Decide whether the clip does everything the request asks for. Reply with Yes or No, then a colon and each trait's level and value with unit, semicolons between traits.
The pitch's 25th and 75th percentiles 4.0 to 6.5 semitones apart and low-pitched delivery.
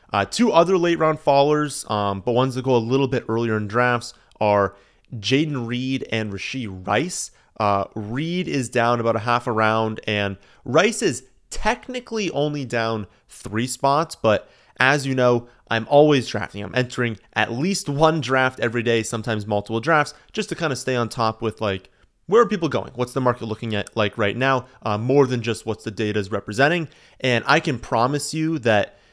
Yes: average, 4.5 semitones; low, 120 Hz